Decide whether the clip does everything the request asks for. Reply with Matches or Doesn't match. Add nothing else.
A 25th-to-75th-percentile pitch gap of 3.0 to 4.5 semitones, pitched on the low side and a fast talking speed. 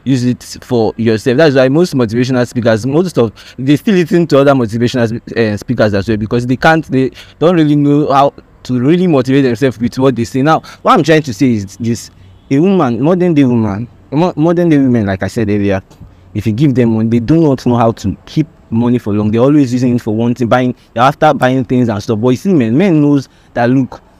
Matches